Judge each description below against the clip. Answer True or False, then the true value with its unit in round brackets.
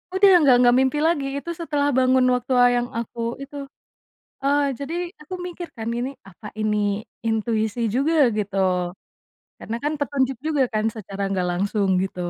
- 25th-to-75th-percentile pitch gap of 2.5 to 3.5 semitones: False (4.9 semitones)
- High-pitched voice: True (250 Hz)